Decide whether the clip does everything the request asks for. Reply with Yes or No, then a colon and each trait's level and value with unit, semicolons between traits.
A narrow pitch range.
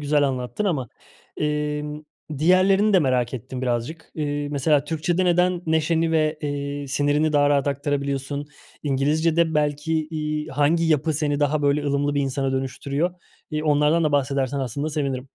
Yes: narrow, 2.0 semitones